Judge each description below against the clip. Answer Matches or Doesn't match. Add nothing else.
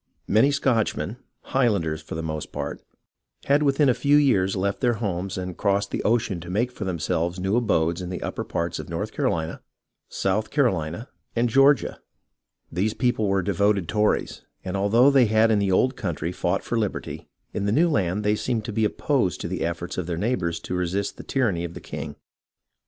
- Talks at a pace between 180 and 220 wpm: Matches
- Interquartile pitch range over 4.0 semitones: Matches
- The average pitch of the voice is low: Matches